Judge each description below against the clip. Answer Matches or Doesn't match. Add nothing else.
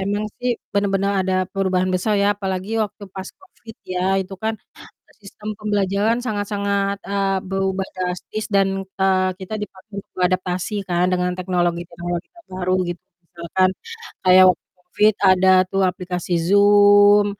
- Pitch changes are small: Matches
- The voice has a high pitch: Matches